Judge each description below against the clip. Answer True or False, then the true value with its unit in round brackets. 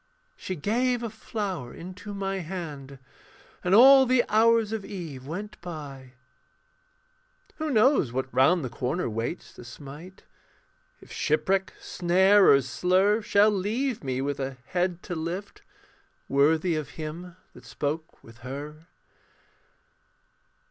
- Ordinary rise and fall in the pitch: False (6.4 semitones)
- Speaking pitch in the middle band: True (175 Hz)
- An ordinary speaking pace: False (130 wpm)